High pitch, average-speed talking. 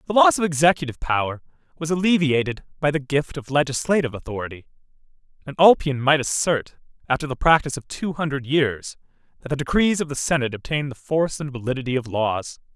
No: medium, 140 Hz; average, 175 wpm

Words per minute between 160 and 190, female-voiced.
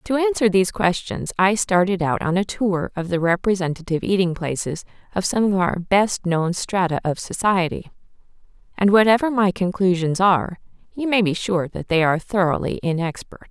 Yes: average, 170 wpm; female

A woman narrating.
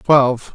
Yes: female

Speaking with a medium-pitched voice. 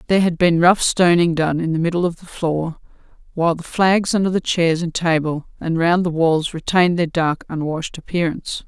Yes: medium, 170 Hz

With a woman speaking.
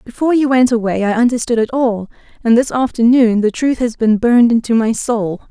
Yes: female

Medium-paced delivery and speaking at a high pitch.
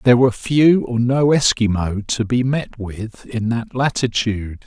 No: average, 165 wpm; low, 120 Hz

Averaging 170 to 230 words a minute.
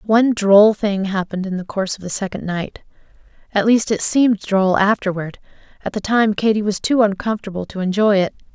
Yes: average, 185 wpm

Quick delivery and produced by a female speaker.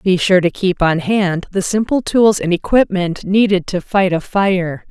No: average, 195 wpm; female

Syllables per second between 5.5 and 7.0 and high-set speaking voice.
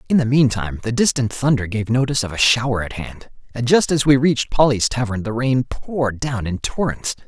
No: 5.6 syllables/s; low, 120 Hz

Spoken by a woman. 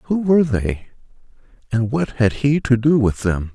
No: male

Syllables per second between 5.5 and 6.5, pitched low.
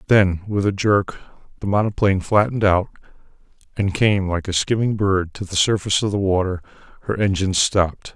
Yes: 5.7 syllables/s; very low, 95 Hz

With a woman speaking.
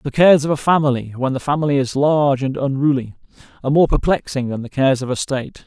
No: male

